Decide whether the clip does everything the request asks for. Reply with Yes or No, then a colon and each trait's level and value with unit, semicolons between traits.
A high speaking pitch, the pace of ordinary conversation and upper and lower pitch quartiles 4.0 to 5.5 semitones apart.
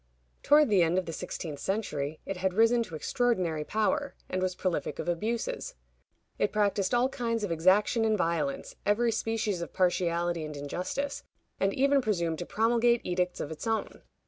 Yes: high, 195 Hz; average, 170 wpm; average, 5.1 semitones